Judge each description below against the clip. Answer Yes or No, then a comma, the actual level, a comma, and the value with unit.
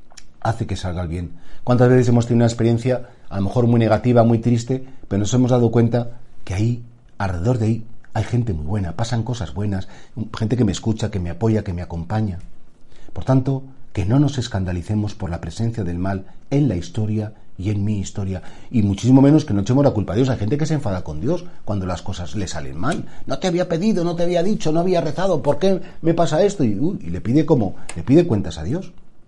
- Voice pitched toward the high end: No, low, 115 Hz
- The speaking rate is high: Yes, fast, 230 wpm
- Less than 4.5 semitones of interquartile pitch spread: No, average, 4.9 semitones